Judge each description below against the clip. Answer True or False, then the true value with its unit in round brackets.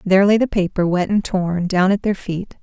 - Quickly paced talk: True (250 wpm)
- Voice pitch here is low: False (190 Hz)